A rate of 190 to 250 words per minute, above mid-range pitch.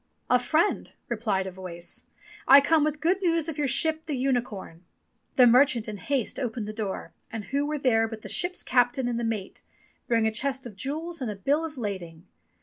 Yes: fast, 205 wpm; high, 245 Hz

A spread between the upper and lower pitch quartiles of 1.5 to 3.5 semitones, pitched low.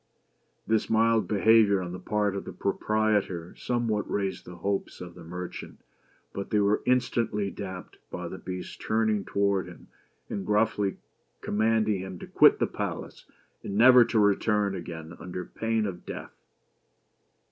Yes: average, 2.8 semitones; low, 100 Hz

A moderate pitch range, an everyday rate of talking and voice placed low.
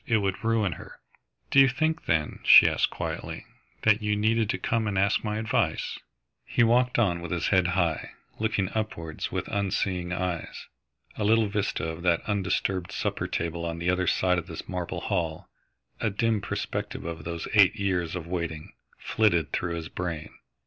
Yes: average, 4.1 semitones; average, 175 wpm; very low, 95 Hz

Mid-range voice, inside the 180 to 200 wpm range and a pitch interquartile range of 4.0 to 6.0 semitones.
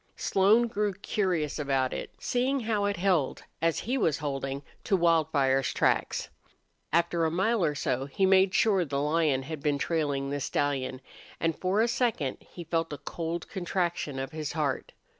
No: medium, 165 Hz; average, 170 wpm; average, 5.2 semitones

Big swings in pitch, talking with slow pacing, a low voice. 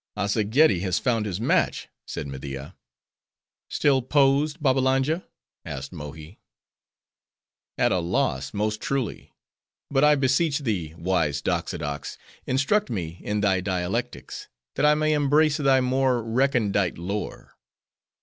Yes: wide, 7.6 semitones; slow, 120 wpm; low, 110 Hz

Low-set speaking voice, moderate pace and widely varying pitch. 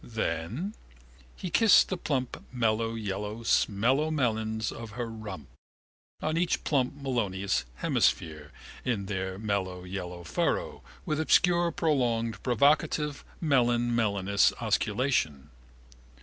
No: low, 115 Hz; slow, 105 wpm; wide, 5.8 semitones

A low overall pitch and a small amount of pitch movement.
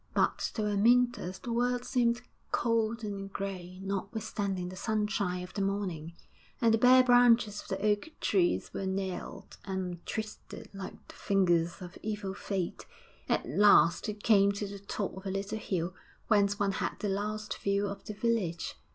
No: high, 200 Hz; narrow, 2.3 semitones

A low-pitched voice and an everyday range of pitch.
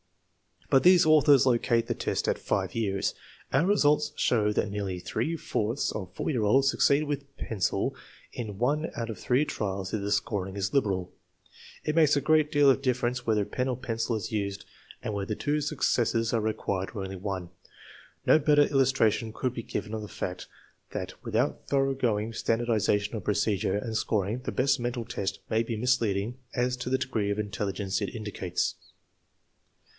Yes: low, 115 Hz; average, 4.7 semitones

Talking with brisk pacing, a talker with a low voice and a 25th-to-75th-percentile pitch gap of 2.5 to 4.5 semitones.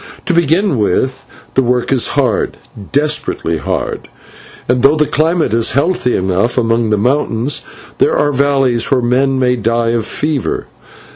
No: average, 150 wpm; low, 125 Hz; average, 3.7 semitones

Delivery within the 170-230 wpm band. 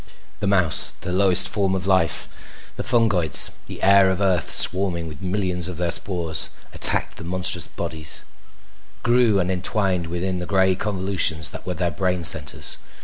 No: average, 160 wpm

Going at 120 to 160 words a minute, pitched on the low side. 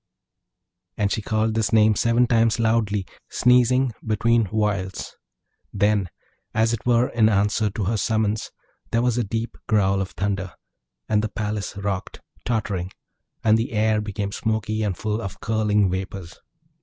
Yes: average, 150 wpm; low, 110 Hz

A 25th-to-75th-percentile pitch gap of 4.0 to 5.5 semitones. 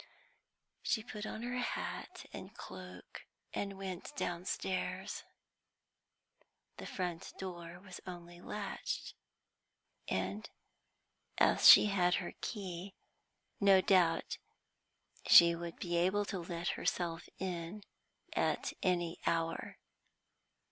No: narrow, 2.5 semitones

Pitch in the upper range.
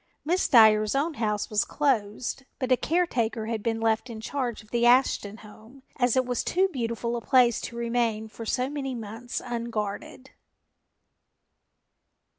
Yes: high, 235 Hz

